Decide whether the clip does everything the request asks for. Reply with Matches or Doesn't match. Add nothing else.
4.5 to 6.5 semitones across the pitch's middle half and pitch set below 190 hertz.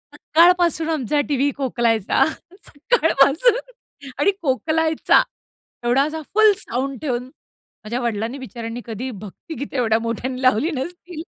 Doesn't match